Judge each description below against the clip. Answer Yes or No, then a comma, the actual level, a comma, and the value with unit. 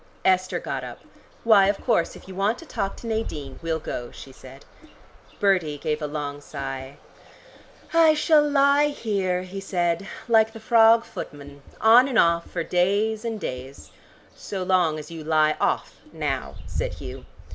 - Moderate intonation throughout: No, wide, 6.6 semitones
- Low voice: No, medium, 185 Hz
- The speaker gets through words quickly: No, average, 170 wpm